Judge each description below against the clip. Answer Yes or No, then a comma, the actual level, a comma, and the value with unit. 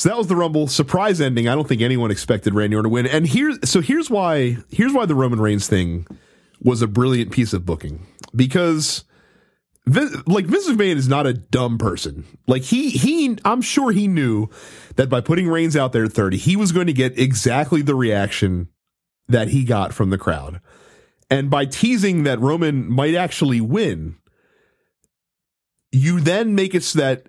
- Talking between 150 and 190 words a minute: Yes, average, 185 wpm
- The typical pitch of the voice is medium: No, low, 130 Hz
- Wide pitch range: Yes, wide, 7.2 semitones